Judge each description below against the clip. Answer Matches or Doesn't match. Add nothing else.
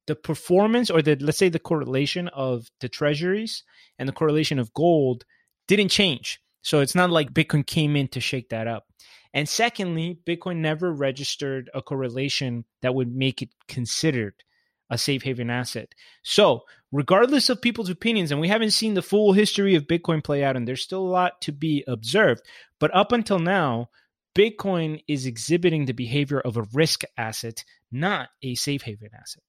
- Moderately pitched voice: Matches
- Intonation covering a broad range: Matches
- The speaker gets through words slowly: Doesn't match